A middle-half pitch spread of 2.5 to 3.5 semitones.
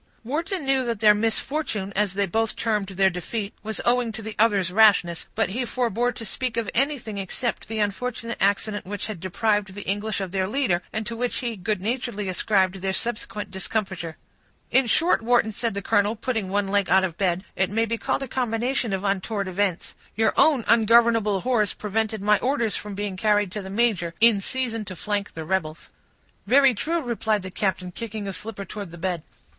Yes: average, 3.2 semitones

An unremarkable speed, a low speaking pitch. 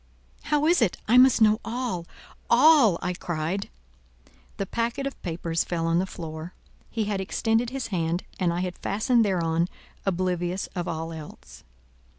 No: average, 155 wpm; medium, 185 Hz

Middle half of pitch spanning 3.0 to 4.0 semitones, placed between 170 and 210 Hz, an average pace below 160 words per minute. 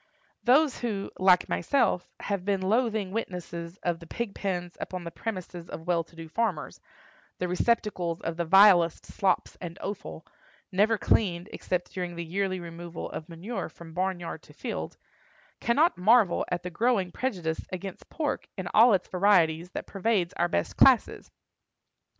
Yes: average, 3.4 semitones; medium, 185 Hz; average, 150 wpm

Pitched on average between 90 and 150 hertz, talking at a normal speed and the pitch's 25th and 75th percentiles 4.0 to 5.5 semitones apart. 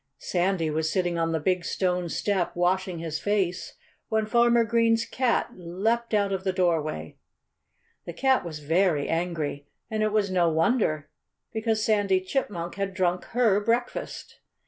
No: medium, 185 Hz; average, 150 wpm; average, 4.3 semitones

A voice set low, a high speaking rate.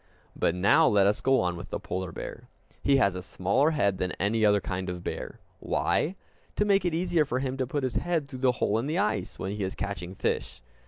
Yes: low, 110 Hz; fast, 235 wpm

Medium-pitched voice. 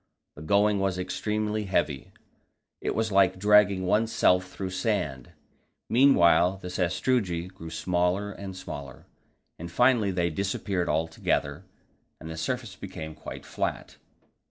No: very low, 95 Hz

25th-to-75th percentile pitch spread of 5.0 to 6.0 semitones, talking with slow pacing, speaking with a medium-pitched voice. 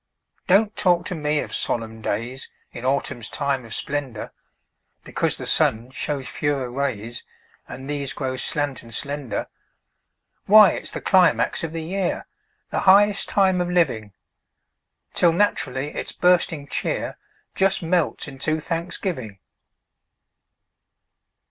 Yes: wide, 5.6 semitones; slow, 125 wpm; medium, 145 Hz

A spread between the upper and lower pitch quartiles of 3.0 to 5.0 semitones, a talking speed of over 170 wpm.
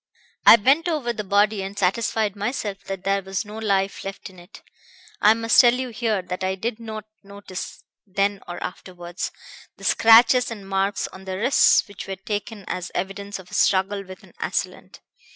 No: narrow, 2.6 semitones; average, 185 wpm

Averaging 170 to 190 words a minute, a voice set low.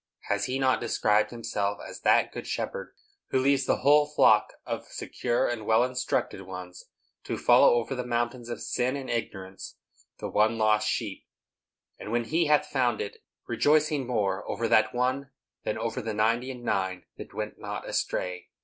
Yes: average, 175 wpm; low, 120 Hz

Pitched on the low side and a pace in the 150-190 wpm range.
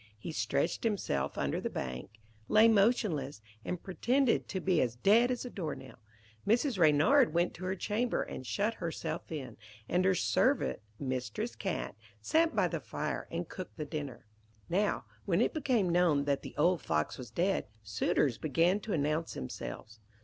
No: medium, 170 Hz; average, 170 wpm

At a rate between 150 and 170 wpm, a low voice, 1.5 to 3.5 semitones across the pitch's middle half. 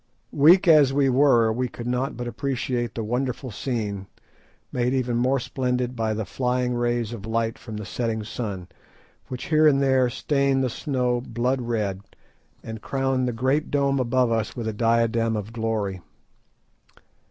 Yes: average, 165 wpm; low, 120 Hz; average, 2.8 semitones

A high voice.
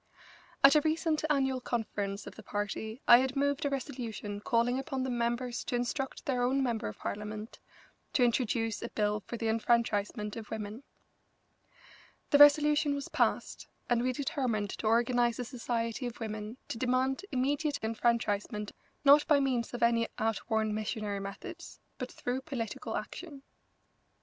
Yes: high, 240 Hz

